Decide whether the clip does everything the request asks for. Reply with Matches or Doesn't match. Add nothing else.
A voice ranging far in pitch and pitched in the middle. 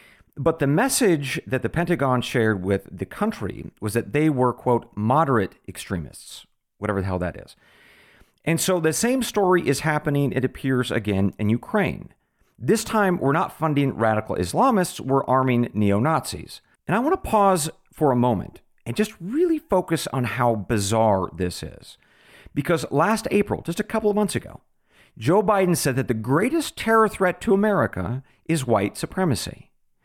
Matches